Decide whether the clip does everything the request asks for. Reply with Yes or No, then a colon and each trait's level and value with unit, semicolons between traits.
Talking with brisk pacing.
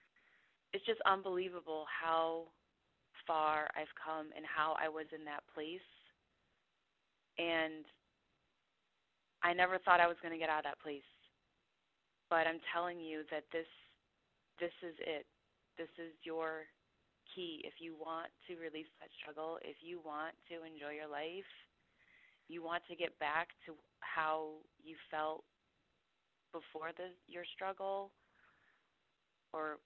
No: slow, 135 wpm